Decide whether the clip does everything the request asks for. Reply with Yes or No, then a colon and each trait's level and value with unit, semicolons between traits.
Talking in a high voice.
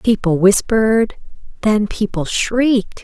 Yes: high, 215 Hz